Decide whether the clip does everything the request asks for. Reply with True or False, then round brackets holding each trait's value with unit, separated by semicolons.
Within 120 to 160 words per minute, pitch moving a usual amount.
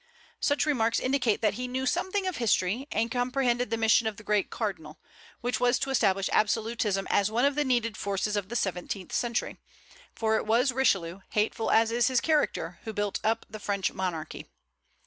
False (185 wpm; 3.4 semitones)